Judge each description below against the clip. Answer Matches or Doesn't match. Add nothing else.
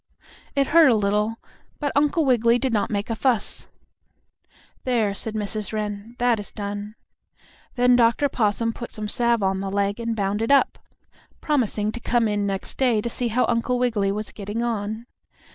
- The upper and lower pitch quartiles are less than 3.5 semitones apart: Matches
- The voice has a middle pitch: Doesn't match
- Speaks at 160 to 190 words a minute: Matches